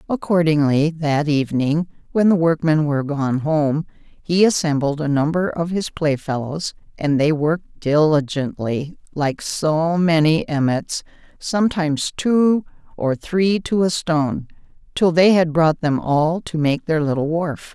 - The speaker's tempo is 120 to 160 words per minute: Yes, average, 140 wpm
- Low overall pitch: No, medium, 160 Hz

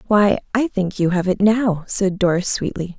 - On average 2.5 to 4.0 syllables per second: No, 4.6 syllables/s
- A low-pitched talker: No, high, 195 Hz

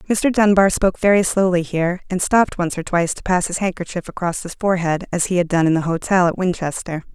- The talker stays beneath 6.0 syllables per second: No, 6.1 syllables/s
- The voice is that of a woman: Yes, female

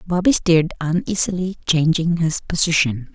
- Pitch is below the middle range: No, medium, 165 Hz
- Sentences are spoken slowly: Yes, slow, 115 wpm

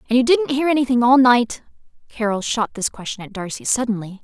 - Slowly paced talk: No, average, 200 wpm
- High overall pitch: Yes, high, 240 Hz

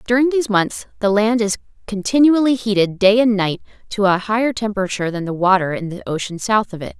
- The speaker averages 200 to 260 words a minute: Yes, fast, 205 wpm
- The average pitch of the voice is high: Yes, high, 210 Hz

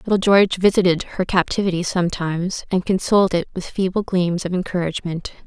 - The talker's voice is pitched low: No, medium, 185 Hz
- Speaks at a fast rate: No, average, 155 wpm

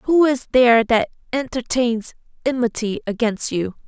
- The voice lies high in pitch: Yes, high, 245 Hz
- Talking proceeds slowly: Yes, slow, 125 wpm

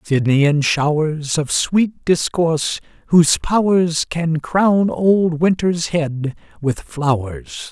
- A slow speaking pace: Yes, slow, 110 wpm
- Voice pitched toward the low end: No, medium, 160 Hz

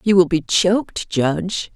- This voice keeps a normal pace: Yes, average, 170 wpm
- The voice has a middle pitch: Yes, medium, 175 Hz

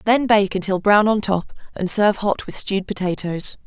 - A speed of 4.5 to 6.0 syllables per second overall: Yes, 5.2 syllables/s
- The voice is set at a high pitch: Yes, high, 200 Hz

